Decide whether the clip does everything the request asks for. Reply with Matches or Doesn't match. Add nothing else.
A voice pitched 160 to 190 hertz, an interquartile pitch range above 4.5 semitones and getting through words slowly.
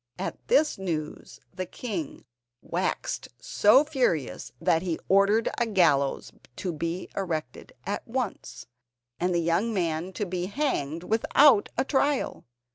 Matches